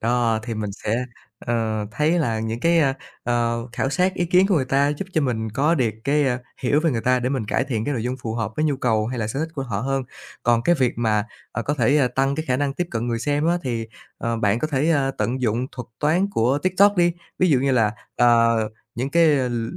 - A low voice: Yes, low, 130 Hz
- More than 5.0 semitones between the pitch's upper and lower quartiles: No, average, 4.2 semitones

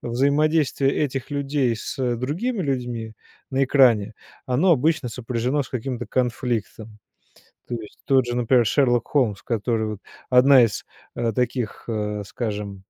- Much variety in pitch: No, average, 3.3 semitones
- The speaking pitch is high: No, low, 125 Hz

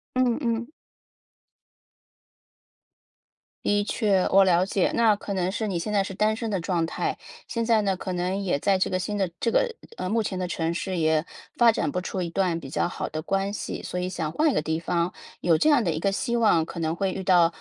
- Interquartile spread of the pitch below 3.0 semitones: No, average, 3.6 semitones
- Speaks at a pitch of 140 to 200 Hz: Yes, high, 190 Hz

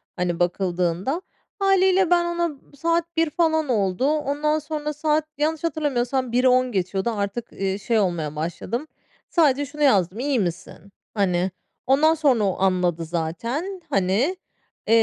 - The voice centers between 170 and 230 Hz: No, very high, 255 Hz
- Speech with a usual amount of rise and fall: No, wide, 8.4 semitones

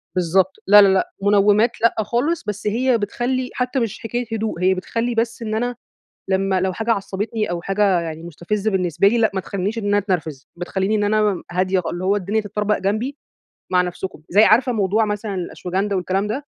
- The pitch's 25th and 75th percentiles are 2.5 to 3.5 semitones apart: Yes, average, 2.9 semitones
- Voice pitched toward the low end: No, high, 205 Hz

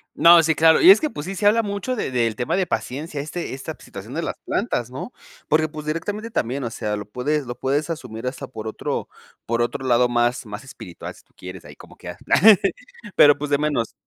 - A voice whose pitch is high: No, medium, 140 Hz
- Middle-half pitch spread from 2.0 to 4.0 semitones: No, average, 5.3 semitones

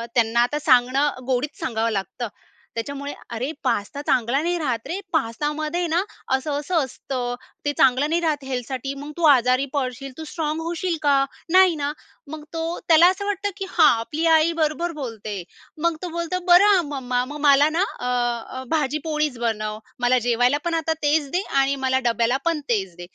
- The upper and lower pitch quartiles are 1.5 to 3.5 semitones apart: No, average, 4.6 semitones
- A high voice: Yes, very high, 285 Hz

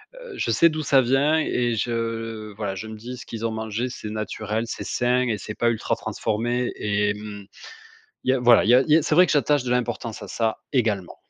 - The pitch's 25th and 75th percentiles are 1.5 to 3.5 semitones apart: Yes, average, 2.8 semitones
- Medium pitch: No, low, 115 Hz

